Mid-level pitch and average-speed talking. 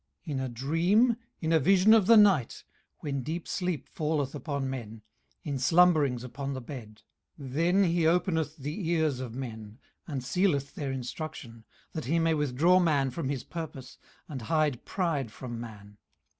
Yes: medium, 145 Hz; average, 170 wpm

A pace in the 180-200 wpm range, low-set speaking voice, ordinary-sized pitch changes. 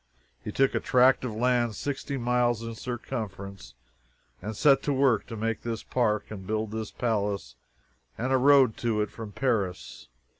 No: average, 165 wpm; low, 115 Hz; average, 3.0 semitones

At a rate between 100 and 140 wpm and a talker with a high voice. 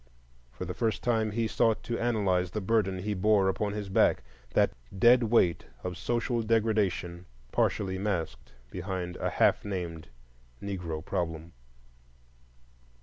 No: slow, 135 wpm; low, 100 Hz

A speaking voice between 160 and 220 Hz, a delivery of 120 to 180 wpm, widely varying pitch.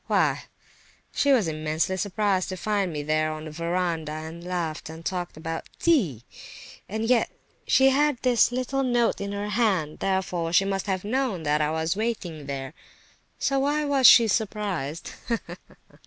Yes: medium, 185 Hz; average, 160 wpm; wide, 6.1 semitones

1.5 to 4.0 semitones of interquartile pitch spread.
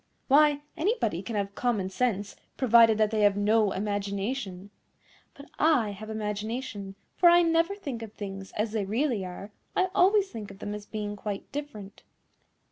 No: average, 5.0 semitones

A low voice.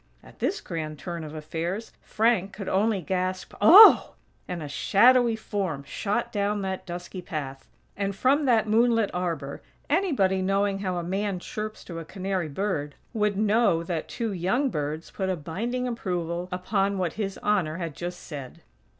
No: high, 190 Hz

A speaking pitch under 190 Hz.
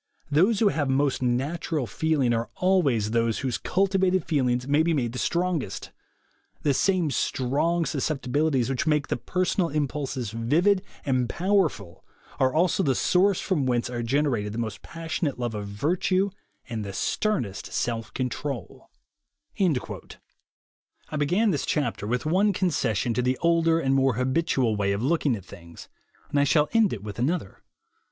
Yes: medium, 140 Hz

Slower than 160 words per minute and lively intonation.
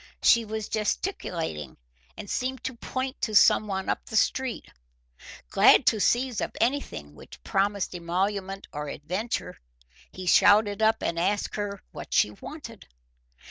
No: average, 140 wpm; average, 3.7 semitones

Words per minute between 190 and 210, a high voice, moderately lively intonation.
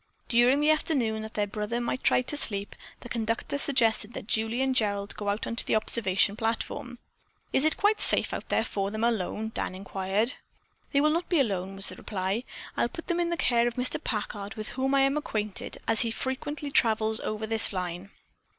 Yes: fast, 205 wpm; high, 225 Hz; average, 4.2 semitones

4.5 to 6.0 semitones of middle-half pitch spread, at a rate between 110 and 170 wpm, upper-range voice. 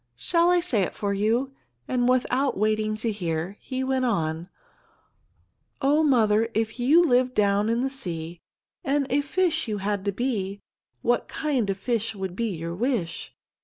Yes: average, 4.8 semitones; average, 165 wpm; high, 225 Hz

